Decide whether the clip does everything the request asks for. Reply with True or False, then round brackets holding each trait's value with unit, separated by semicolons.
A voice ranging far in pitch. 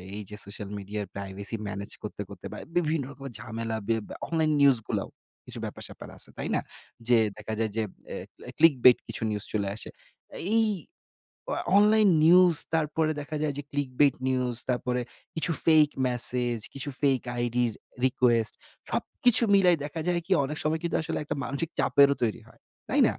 True (5.7 semitones)